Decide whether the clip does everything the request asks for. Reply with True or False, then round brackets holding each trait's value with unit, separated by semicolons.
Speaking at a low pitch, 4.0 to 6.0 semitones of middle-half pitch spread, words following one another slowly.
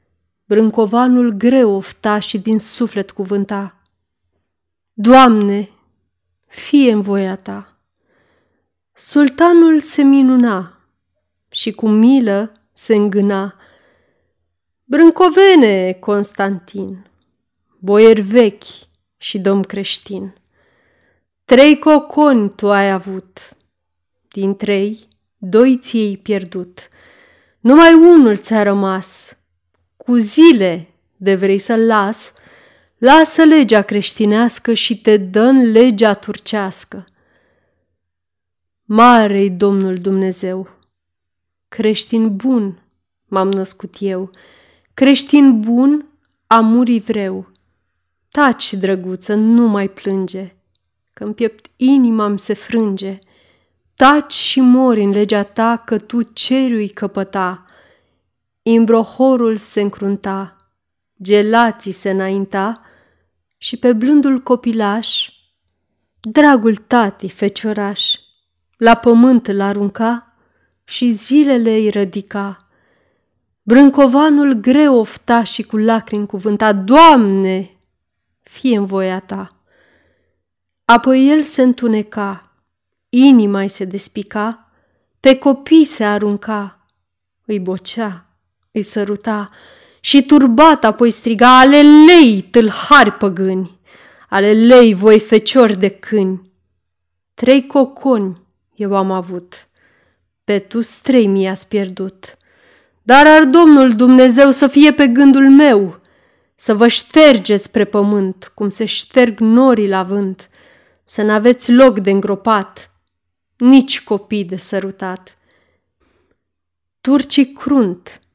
False (210 Hz; 4.3 semitones; 100 wpm)